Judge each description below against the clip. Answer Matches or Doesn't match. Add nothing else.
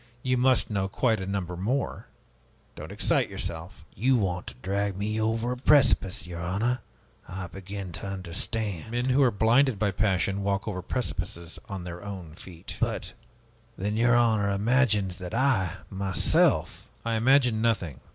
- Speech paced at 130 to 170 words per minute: Matches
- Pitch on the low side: Matches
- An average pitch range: Matches